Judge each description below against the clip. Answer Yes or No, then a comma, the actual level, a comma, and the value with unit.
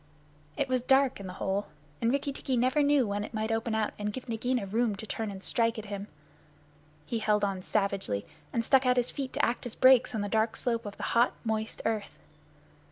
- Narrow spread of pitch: No, average, 3.3 semitones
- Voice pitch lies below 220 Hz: No, high, 225 Hz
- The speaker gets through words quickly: Yes, fast, 225 wpm